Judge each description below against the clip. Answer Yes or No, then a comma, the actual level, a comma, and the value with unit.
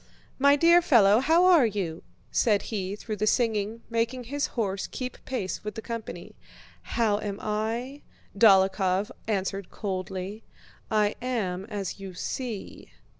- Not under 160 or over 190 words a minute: No, slow, 135 wpm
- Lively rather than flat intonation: No, average, 3.5 semitones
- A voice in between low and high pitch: No, high, 215 Hz